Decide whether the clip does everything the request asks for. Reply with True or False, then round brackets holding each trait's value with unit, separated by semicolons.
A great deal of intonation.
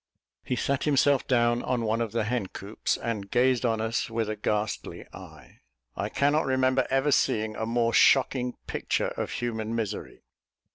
False (2.8 semitones)